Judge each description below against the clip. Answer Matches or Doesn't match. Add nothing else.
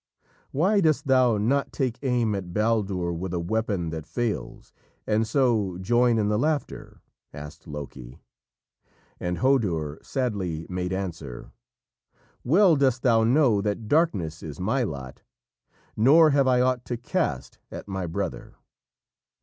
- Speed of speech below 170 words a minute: Matches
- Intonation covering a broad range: Matches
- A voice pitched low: Matches